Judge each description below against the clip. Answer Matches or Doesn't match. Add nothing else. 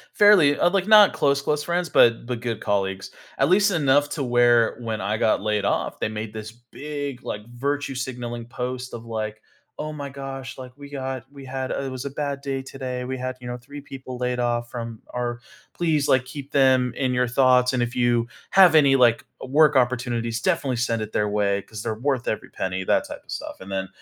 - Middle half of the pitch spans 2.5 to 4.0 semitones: Matches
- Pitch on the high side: Doesn't match